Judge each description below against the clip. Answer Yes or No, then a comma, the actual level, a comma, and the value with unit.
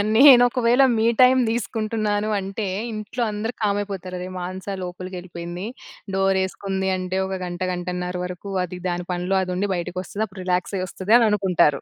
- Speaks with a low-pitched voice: No, high, 190 Hz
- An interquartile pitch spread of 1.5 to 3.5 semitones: Yes, average, 2.7 semitones